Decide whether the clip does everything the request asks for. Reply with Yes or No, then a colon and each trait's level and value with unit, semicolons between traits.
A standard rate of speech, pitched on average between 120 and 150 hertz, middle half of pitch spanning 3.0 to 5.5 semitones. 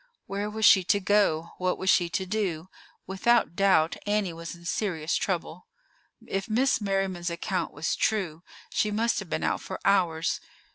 No: average, 165 wpm; high, 190 Hz; average, 3.4 semitones